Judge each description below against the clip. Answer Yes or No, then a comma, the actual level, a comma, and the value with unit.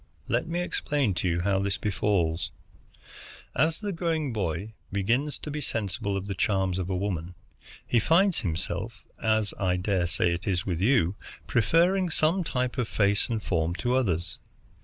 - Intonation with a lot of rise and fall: Yes, wide, 6.6 semitones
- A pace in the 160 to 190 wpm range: Yes, average, 165 wpm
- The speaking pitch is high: No, low, 100 Hz